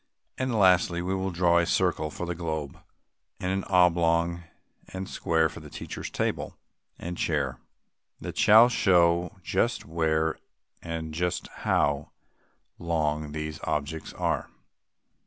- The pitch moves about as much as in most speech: No, narrow, 2.3 semitones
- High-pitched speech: No, very low, 85 Hz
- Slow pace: Yes, slow, 130 wpm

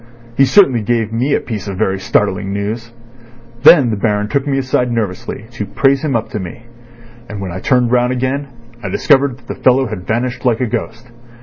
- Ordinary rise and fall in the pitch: Yes, average, 3.7 semitones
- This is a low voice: Yes, low, 120 Hz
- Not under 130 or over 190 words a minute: No, fast, 205 wpm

